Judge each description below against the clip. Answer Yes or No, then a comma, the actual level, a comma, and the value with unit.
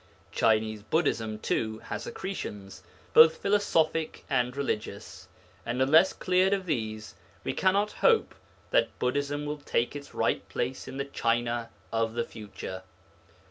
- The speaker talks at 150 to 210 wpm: No, slow, 135 wpm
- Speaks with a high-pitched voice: No, low, 130 Hz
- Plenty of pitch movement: Yes, wide, 6.3 semitones